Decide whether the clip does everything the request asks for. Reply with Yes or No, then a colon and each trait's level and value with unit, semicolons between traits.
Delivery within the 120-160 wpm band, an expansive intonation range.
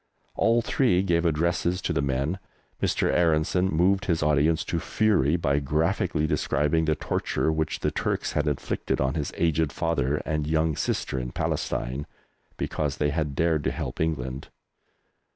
No: average, 155 wpm; average, 2.7 semitones